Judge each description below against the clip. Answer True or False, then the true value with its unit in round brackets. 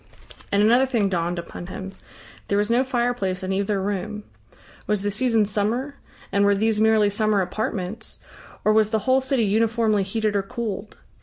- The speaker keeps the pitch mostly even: True (2.3 semitones)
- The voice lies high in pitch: True (210 Hz)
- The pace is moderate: True (170 wpm)